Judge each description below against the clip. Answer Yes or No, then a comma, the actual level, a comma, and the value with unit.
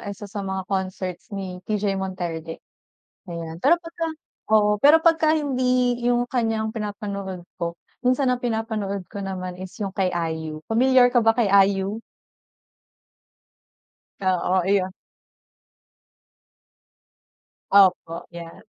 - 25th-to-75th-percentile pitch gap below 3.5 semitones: No, average, 4.6 semitones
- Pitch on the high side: Yes, high, 200 Hz